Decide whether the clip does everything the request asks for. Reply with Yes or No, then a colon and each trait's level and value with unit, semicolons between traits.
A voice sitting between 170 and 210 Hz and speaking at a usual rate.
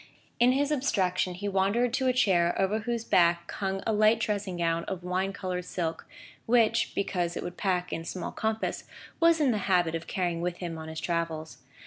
Yes: high, 190 Hz; average, 195 wpm